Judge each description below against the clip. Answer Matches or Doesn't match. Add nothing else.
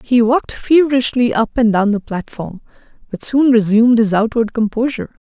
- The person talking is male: Doesn't match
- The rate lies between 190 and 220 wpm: Doesn't match